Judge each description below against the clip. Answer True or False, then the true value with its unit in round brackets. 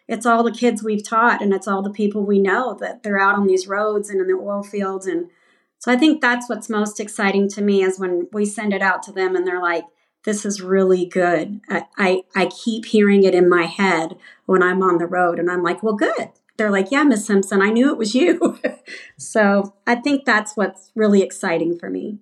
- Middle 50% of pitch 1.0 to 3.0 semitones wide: True (2.7 semitones)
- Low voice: False (200 Hz)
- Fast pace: True (235 wpm)